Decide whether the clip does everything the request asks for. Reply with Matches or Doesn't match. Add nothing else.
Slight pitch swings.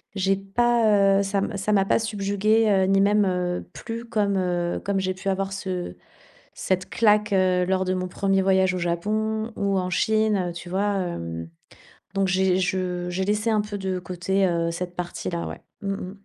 Matches